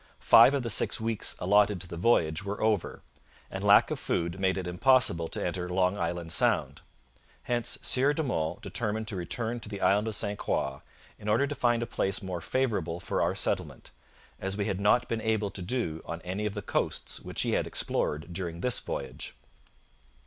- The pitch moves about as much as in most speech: Yes, average, 4.4 semitones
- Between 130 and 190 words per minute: No, average, 200 wpm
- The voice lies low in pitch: Yes, low, 100 Hz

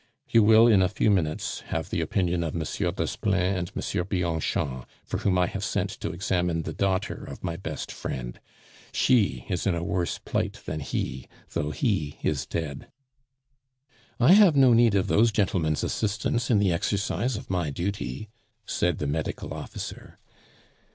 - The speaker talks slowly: No, average, 165 wpm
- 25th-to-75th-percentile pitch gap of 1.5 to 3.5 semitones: No, average, 4.4 semitones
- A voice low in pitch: Yes, very low, 90 Hz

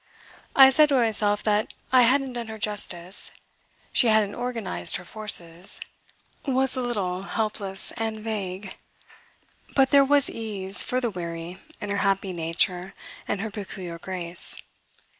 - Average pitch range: Yes, average, 4.2 semitones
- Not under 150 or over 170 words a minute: No, average, 140 wpm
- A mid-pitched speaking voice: No, high, 210 Hz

